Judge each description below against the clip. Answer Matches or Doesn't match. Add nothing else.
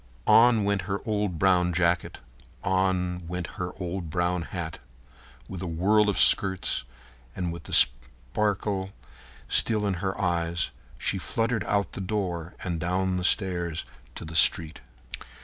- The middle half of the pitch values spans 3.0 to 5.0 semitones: Doesn't match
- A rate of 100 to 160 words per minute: Matches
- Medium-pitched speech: Doesn't match